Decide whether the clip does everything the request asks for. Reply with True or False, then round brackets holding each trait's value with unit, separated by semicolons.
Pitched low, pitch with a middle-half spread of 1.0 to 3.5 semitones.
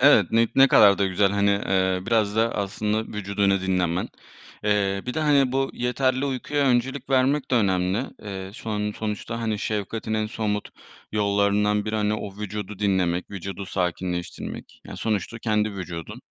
True (105 Hz; 2.7 semitones)